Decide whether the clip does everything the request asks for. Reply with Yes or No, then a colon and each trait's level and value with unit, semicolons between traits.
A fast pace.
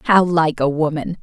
No: average, 195 wpm